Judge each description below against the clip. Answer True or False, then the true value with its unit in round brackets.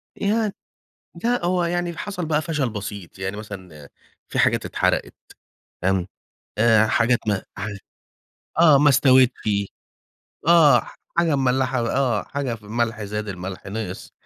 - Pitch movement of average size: False (6.7 semitones)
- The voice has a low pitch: True (120 Hz)